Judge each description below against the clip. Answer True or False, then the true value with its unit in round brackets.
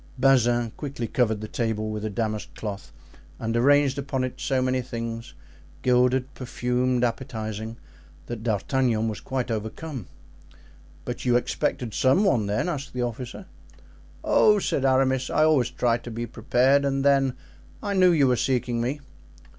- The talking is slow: False (155 wpm)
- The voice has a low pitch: True (125 Hz)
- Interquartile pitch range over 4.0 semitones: False (2.8 semitones)